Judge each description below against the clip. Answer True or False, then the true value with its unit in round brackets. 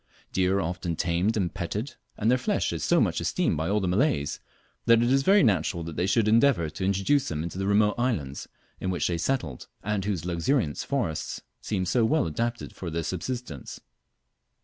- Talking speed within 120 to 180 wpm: False (190 wpm)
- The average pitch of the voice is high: False (95 Hz)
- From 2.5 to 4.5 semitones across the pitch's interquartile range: False (5.6 semitones)